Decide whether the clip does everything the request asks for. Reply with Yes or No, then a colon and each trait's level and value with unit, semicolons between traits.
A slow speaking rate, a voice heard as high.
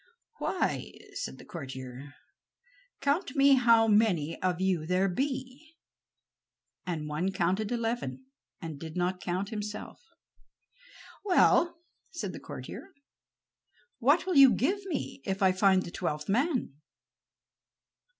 Yes: slow, 120 wpm; high, 195 Hz